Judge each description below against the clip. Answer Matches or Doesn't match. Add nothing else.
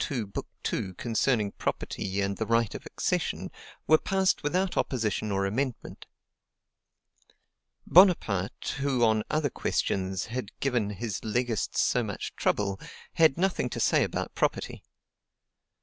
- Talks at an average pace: Doesn't match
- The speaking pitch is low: Matches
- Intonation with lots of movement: Matches